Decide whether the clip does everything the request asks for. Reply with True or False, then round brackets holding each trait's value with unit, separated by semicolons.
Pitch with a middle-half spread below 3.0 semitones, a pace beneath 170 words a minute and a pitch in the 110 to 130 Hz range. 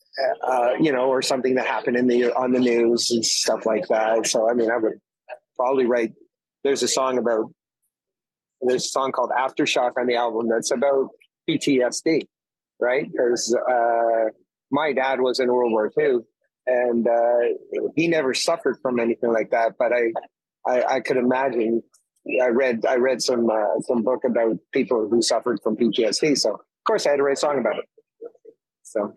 False (2.5 semitones; 185 wpm; 125 Hz)